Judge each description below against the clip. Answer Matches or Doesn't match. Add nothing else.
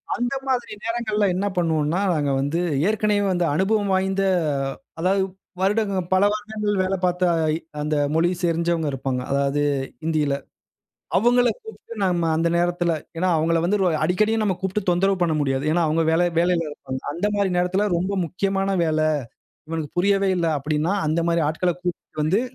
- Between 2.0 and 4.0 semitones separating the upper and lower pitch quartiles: Matches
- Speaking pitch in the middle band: Matches